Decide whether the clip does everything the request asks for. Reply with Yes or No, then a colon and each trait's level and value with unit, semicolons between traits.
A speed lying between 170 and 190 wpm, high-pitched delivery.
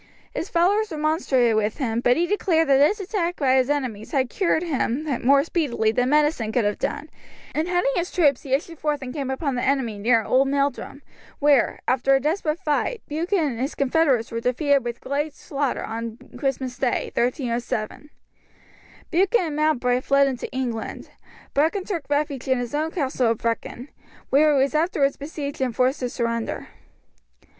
Yes: average, 175 wpm; very high, 275 Hz